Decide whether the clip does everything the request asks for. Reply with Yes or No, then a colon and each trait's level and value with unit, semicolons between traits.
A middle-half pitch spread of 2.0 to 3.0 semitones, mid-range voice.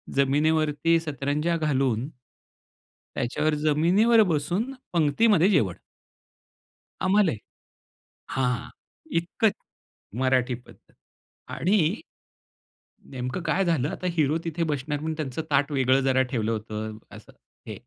No: average, 4.3 semitones; medium, 150 Hz